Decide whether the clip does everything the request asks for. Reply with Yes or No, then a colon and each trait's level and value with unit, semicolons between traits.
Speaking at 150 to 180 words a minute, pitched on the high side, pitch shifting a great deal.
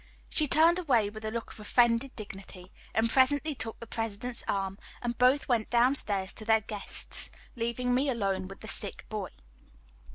No: average, 175 wpm; high, 230 Hz; average, 3.4 semitones